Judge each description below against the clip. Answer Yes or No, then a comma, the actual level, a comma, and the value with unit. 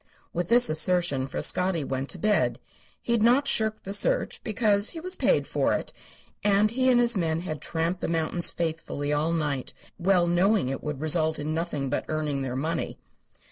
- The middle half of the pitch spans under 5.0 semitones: No, average, 5.3 semitones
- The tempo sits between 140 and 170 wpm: No, average, 185 wpm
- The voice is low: No, medium, 170 Hz